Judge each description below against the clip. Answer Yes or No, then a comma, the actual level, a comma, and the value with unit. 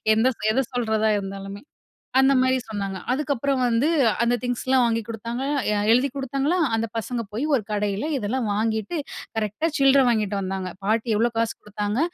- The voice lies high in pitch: Yes, high, 230 Hz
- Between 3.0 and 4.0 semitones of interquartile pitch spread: Yes, average, 3.7 semitones